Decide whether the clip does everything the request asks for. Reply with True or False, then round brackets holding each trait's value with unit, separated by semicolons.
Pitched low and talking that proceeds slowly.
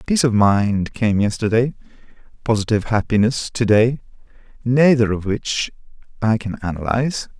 True (110 Hz; 120 wpm)